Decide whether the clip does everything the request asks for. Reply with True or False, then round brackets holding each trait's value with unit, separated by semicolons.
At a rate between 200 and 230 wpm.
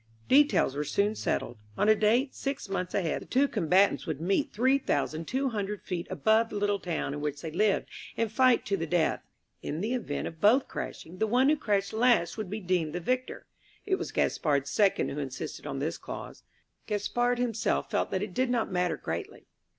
True (205 wpm)